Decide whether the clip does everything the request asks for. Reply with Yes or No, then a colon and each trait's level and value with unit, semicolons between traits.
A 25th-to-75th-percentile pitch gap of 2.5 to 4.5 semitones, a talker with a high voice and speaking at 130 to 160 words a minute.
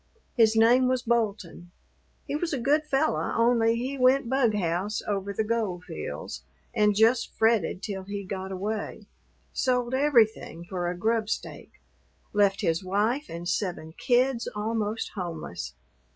Yes: average, 4.1 semitones; high, 220 Hz; average, 140 wpm